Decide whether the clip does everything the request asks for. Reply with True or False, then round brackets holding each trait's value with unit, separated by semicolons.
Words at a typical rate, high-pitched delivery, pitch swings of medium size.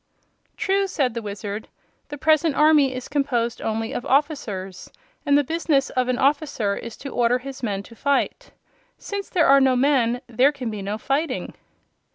True (175 wpm; 265 Hz; 4.0 semitones)